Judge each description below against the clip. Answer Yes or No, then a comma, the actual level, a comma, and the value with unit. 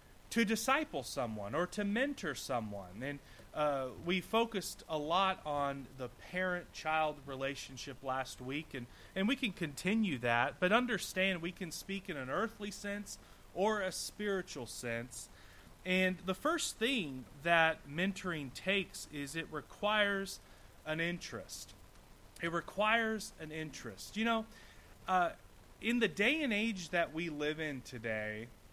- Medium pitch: Yes, medium, 170 Hz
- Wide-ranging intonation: Yes, wide, 7.2 semitones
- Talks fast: No, average, 140 wpm